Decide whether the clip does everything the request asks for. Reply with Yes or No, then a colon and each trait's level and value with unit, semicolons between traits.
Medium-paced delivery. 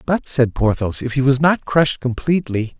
Yes: average, 195 wpm